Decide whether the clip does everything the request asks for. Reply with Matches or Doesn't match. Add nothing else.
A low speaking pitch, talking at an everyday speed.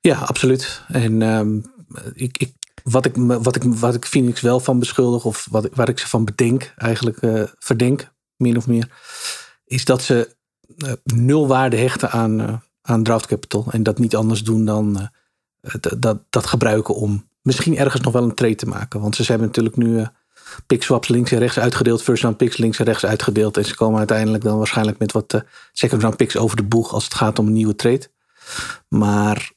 Doesn't match